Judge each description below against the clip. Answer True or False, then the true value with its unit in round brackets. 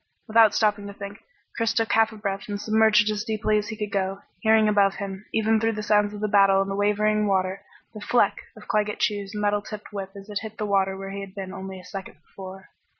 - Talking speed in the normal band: False (240 wpm)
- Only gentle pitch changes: True (1.5 semitones)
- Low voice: False (205 Hz)